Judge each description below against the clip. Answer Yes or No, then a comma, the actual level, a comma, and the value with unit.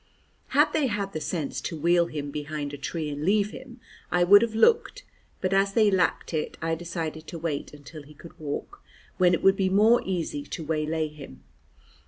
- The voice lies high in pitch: No, medium, 170 Hz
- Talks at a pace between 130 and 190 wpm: No, average, 200 wpm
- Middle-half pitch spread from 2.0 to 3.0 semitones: No, average, 4.5 semitones